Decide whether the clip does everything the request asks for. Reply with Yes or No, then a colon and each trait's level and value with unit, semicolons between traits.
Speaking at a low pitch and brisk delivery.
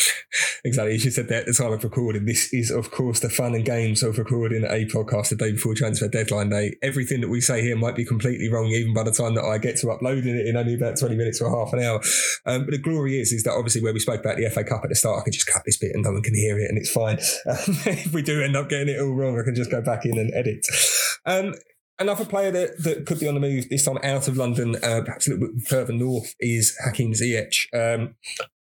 Yes: low, 120 Hz; fast, 275 wpm